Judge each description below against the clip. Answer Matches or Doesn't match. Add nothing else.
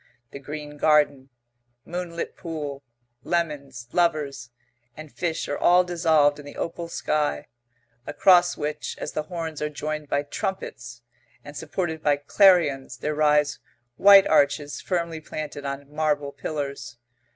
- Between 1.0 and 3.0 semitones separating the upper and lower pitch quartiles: Matches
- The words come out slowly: Matches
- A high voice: Doesn't match